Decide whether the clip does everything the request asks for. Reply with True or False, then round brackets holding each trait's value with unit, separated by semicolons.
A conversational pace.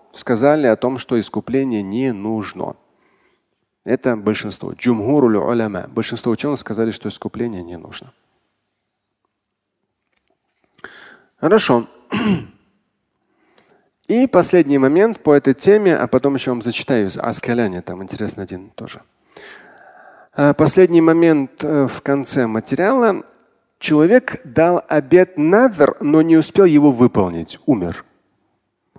False (100 wpm)